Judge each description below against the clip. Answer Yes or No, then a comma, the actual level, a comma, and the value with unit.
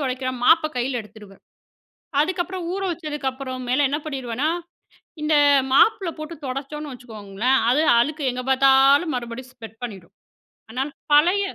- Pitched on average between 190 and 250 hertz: No, very high, 270 Hz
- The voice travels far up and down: No, average, 3.7 semitones